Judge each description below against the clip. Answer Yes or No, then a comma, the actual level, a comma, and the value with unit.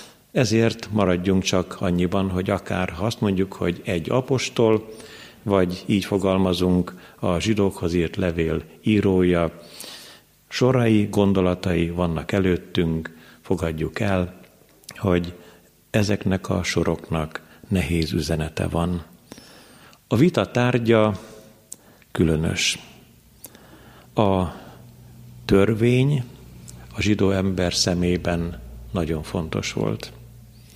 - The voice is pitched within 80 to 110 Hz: Yes, very low, 95 Hz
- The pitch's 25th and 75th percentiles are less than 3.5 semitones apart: No, average, 3.9 semitones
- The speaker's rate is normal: No, slow, 90 wpm